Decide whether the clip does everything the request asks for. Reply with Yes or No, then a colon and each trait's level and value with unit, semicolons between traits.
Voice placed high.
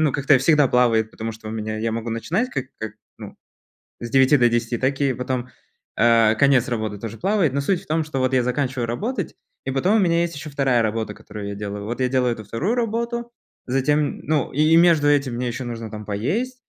No: low, 130 Hz